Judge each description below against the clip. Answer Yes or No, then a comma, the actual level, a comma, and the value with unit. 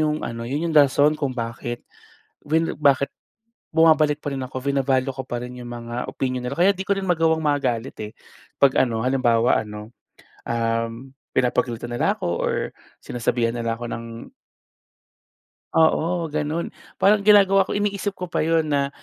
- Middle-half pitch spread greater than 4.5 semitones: Yes, average, 5.1 semitones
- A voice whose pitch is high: No, low, 135 Hz